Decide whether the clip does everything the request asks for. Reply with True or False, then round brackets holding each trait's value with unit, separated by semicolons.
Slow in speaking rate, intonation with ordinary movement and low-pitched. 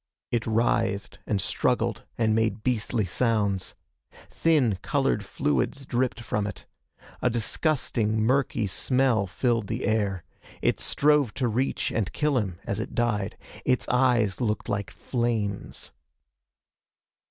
True (125 wpm; 3.4 semitones; 115 Hz)